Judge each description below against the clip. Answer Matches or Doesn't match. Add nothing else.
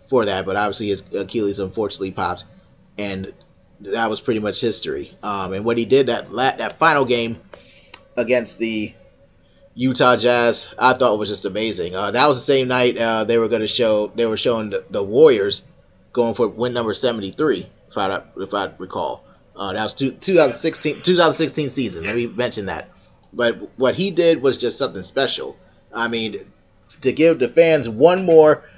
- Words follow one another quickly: Doesn't match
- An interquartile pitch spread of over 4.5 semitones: Matches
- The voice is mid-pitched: Doesn't match